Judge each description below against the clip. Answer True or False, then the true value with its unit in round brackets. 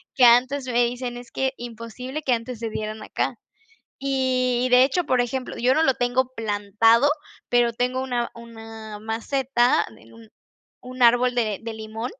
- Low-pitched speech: False (245 Hz)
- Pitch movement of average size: False (2.1 semitones)